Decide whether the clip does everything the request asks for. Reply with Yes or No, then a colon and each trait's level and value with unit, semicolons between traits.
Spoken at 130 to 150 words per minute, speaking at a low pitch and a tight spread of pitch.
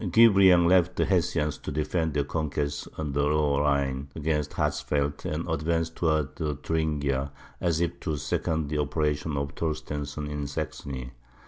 Yes: average, 145 wpm; very low, 75 Hz; narrow, 2.2 semitones